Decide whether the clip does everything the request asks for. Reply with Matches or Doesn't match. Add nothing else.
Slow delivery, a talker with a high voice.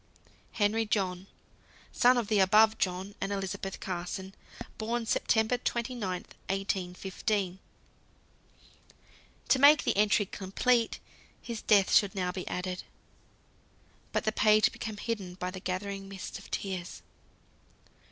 Matches